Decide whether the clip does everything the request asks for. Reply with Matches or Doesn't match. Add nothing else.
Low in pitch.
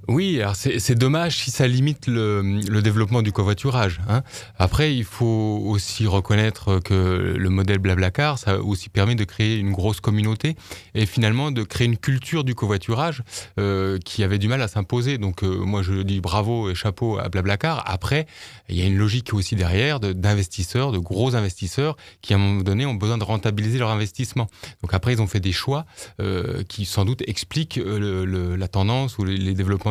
Matches